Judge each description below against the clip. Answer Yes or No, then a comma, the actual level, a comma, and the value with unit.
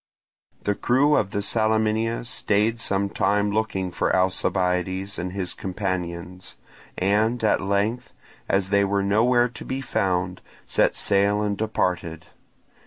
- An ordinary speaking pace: No, slow, 130 wpm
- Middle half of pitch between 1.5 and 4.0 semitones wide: Yes, average, 2.8 semitones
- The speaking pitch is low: Yes, low, 100 Hz